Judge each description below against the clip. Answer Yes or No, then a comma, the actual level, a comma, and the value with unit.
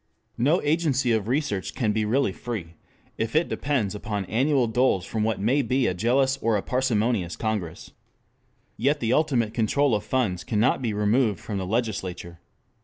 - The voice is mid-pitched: No, low, 115 Hz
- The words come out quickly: No, average, 170 wpm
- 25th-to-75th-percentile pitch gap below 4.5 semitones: Yes, average, 4.1 semitones